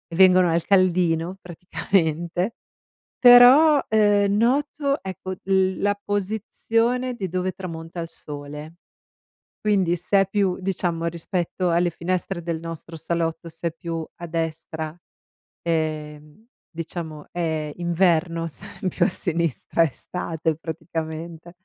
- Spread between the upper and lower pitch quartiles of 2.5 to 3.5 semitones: Yes, average, 2.9 semitones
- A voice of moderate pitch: Yes, medium, 170 Hz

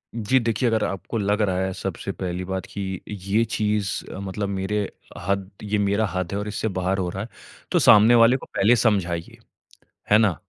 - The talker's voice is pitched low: Yes, low, 100 Hz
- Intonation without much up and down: Yes, narrow, 2.3 semitones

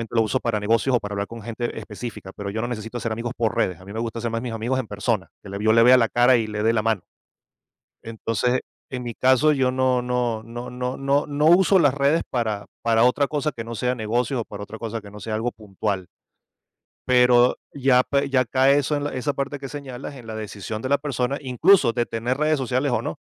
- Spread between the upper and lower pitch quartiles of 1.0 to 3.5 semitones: Yes, average, 2.9 semitones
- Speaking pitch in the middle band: No, low, 120 Hz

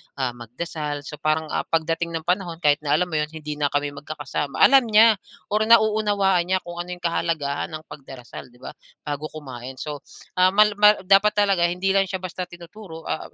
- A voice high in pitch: No, medium, 170 Hz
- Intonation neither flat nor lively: Yes, average, 4.6 semitones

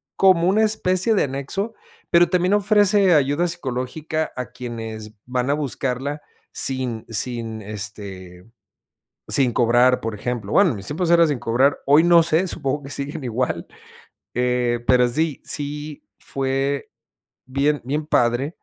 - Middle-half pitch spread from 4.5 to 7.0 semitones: Yes, average, 4.9 semitones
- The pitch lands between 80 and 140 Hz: Yes, low, 135 Hz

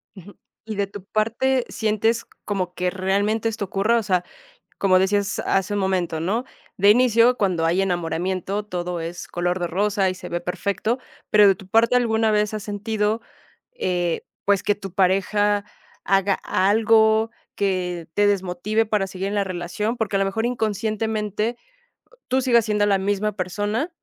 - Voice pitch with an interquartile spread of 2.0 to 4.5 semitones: Yes, average, 2.7 semitones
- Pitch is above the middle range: Yes, high, 205 Hz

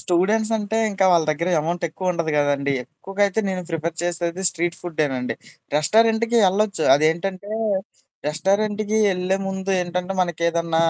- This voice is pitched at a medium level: Yes, medium, 180 Hz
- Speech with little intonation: No, average, 3.1 semitones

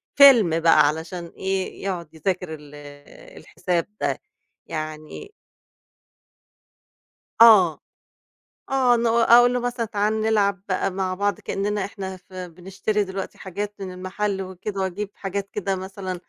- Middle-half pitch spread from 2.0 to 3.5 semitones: Yes, narrow, 2.5 semitones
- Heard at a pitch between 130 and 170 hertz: No, high, 195 Hz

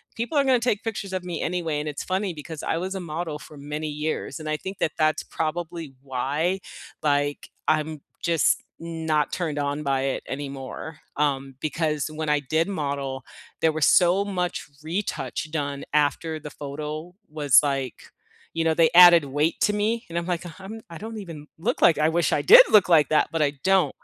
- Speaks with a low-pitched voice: No, medium, 160 Hz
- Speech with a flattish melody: No, average, 3.2 semitones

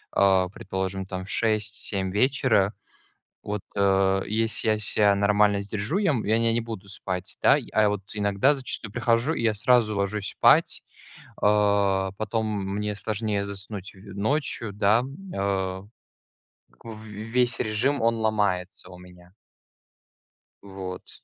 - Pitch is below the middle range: Yes, low, 105 Hz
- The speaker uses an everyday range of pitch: No, narrow, 2.2 semitones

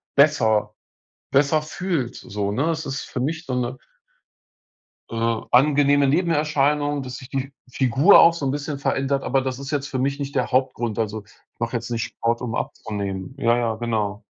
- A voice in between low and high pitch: No, low, 130 Hz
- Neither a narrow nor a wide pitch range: Yes, average, 3.7 semitones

